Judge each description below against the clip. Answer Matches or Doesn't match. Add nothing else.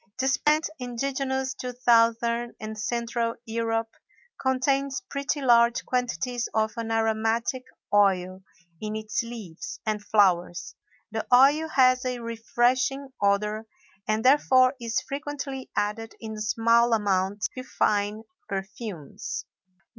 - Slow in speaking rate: Matches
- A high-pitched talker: Matches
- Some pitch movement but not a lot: Matches